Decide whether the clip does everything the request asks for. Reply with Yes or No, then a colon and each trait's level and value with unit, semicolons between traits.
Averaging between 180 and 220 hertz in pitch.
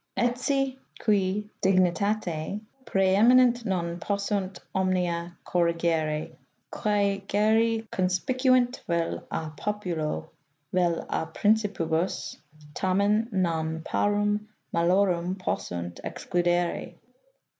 Yes: high, 190 Hz